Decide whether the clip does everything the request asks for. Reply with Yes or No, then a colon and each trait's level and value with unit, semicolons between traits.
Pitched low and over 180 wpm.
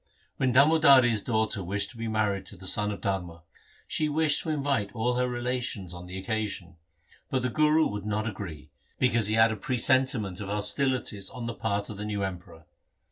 Yes: low, 110 Hz; average, 190 wpm